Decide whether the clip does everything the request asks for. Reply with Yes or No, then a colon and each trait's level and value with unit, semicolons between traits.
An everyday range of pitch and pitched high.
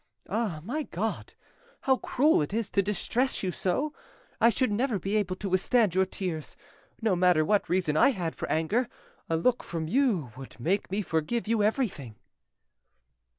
No: wide, 5.7 semitones; high, 195 Hz